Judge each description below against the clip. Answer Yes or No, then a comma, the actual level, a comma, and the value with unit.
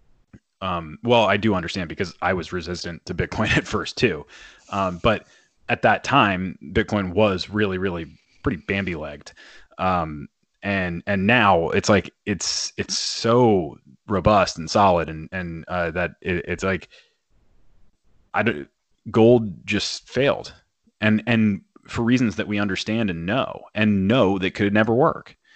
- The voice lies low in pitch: Yes, very low, 95 Hz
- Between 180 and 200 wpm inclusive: No, average, 155 wpm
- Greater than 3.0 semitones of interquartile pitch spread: Yes, average, 3.5 semitones